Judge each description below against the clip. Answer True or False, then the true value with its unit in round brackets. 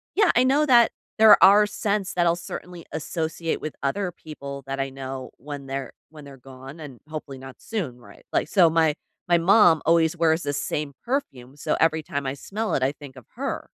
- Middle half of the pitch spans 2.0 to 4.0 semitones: False (4.7 semitones)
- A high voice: False (155 Hz)